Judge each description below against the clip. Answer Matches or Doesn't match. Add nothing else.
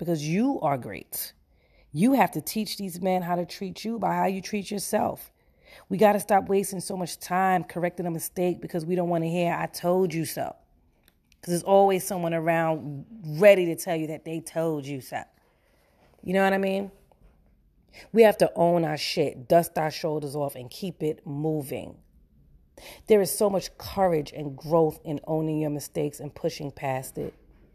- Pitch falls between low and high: Matches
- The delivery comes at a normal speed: Matches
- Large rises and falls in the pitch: Doesn't match